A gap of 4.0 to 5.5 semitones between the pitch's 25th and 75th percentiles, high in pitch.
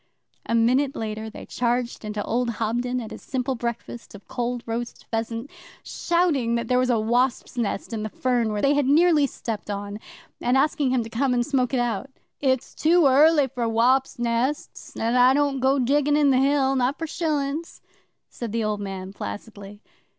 No: average, 3.2 semitones; high, 245 Hz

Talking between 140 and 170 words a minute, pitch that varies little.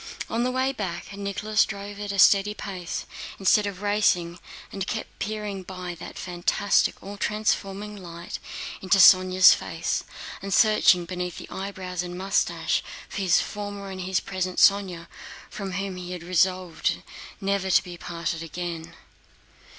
Yes: average, 150 wpm; narrow, 2.1 semitones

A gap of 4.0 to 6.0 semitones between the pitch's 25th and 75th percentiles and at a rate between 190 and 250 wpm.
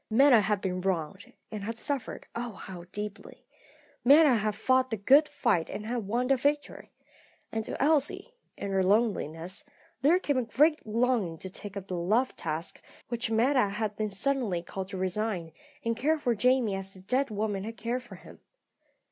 No: average, 4.9 semitones; average, 180 wpm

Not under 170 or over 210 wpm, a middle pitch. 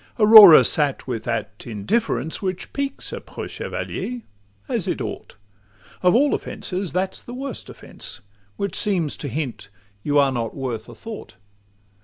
No: average, 150 wpm; medium, 155 Hz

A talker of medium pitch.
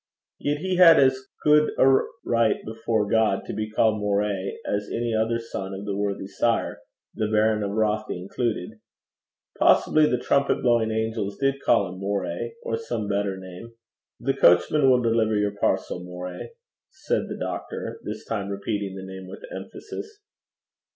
No: low, 110 Hz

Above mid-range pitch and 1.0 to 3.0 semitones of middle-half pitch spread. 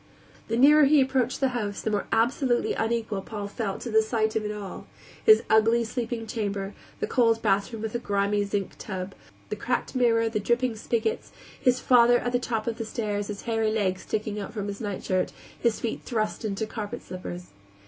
Yes: high, 220 Hz; narrow, 2.6 semitones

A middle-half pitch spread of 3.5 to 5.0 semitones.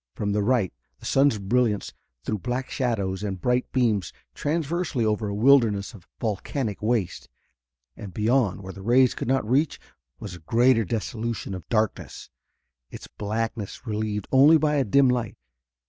Yes: average, 3.9 semitones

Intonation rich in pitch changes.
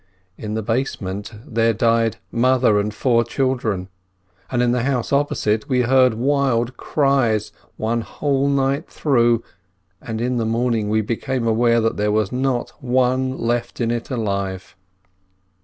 No: average, 2.7 semitones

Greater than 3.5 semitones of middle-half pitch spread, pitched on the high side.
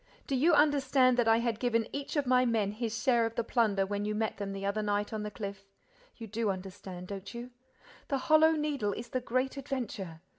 Yes: average, 3.9 semitones; high, 230 Hz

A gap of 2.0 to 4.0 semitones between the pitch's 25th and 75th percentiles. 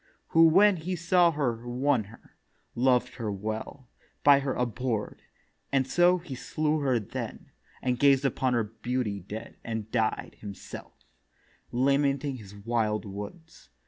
No: average, 4.5 semitones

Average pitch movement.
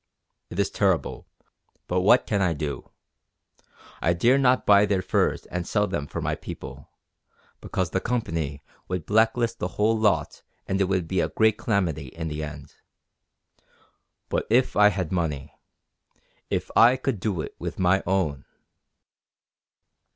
Yes: average, 4.7 semitones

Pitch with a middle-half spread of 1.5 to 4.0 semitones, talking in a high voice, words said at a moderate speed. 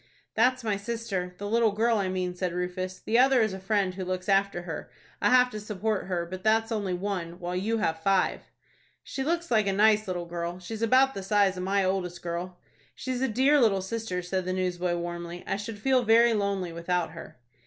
No: average, 3.7 semitones; high, 195 Hz; fast, 215 wpm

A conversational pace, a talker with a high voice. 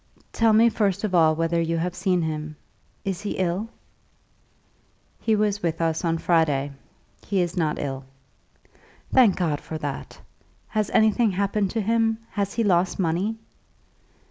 No: average, 150 wpm; medium, 180 Hz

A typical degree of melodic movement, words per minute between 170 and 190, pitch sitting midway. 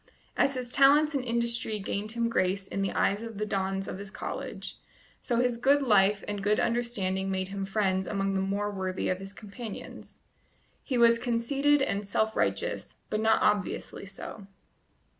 No: average, 3.3 semitones; average, 175 wpm; high, 210 Hz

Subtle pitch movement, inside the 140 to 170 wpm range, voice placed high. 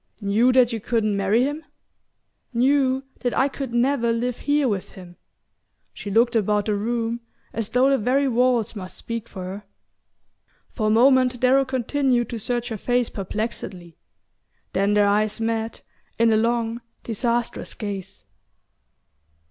No: average, 3.1 semitones; average, 150 wpm; high, 230 Hz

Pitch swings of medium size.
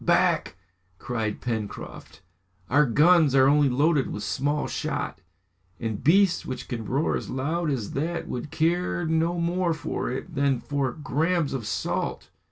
Yes: average, 4.4 semitones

